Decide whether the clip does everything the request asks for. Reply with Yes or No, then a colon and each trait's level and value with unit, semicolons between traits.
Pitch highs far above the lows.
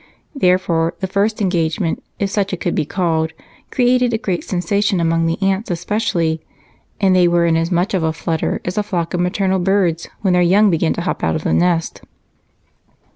No: average, 3.0 semitones